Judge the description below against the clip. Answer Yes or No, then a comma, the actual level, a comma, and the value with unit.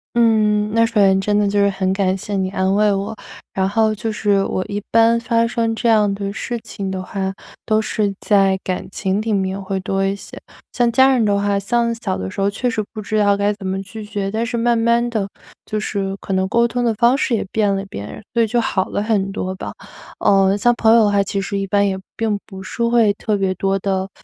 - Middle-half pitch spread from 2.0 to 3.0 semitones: Yes, narrow, 2.5 semitones